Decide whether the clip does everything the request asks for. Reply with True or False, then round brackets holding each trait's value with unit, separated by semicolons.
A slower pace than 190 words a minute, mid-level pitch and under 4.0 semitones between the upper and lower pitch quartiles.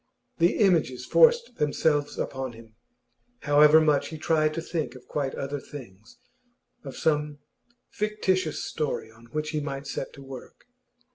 True (145 wpm; 145 Hz; 3.0 semitones)